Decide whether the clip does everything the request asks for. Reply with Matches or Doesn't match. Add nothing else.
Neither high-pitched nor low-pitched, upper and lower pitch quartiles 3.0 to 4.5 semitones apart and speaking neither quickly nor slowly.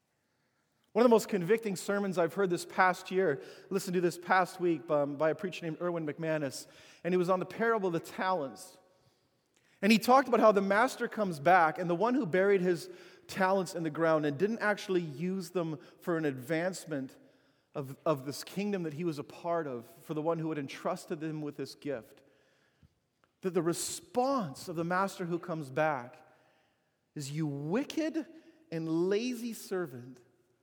Matches